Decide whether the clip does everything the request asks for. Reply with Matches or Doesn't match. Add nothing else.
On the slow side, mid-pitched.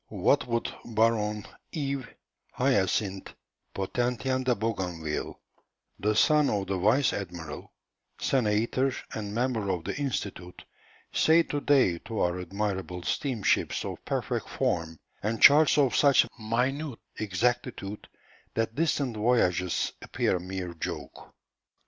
Doesn't match